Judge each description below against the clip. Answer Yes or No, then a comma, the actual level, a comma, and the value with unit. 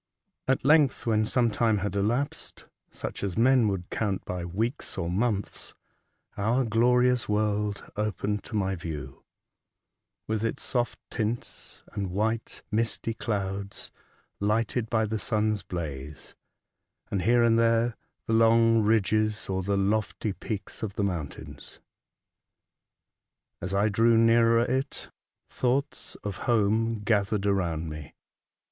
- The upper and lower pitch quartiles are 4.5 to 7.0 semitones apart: No, average, 2.7 semitones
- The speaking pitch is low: Yes, low, 110 Hz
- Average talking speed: No, slow, 130 wpm